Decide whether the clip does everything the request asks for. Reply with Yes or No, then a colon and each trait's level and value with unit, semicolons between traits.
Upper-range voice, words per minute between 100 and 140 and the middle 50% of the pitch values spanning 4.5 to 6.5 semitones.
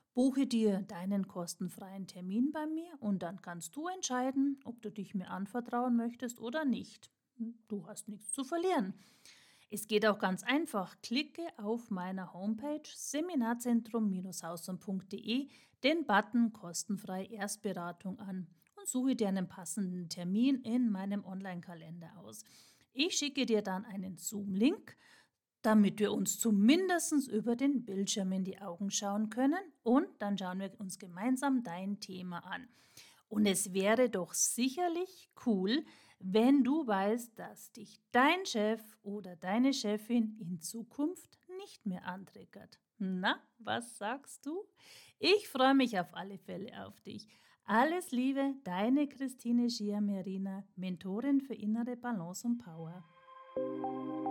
Yes: high, 215 Hz; average, 135 wpm; average, 5.1 semitones